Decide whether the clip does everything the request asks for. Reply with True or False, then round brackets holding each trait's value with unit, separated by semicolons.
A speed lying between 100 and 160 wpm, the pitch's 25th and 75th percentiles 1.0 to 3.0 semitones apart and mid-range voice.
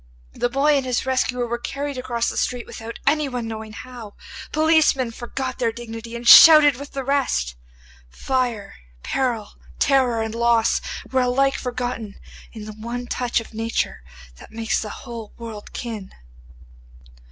False (150 wpm; 2.5 semitones; 240 Hz)